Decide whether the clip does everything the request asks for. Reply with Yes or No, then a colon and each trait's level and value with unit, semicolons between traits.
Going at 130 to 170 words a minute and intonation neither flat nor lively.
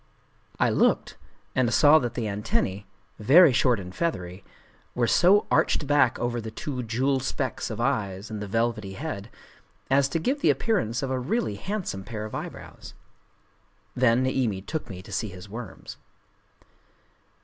Yes: average, 160 wpm; average, 4.9 semitones